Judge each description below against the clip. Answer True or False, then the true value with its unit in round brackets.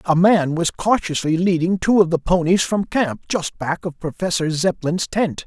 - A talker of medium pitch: True (170 Hz)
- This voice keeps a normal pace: True (185 wpm)